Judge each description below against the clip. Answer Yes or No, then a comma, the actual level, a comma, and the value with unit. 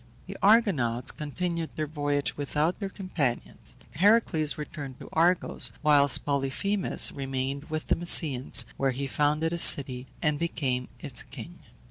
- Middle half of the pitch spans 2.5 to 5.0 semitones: Yes, average, 3.6 semitones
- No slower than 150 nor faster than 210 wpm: No, slow, 135 wpm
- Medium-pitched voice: Yes, medium, 150 Hz